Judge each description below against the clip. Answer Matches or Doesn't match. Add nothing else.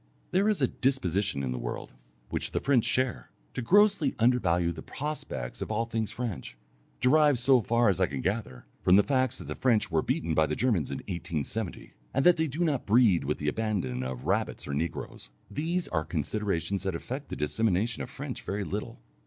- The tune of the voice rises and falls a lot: Matches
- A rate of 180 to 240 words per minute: Matches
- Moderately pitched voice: Doesn't match